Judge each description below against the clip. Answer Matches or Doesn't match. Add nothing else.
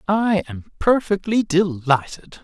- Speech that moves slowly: Matches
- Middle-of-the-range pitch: Matches